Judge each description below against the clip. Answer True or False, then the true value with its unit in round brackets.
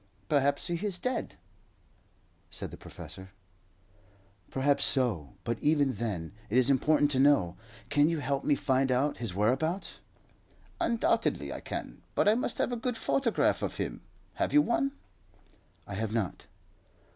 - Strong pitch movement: True (6.3 semitones)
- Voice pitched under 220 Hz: True (140 Hz)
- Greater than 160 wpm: False (155 wpm)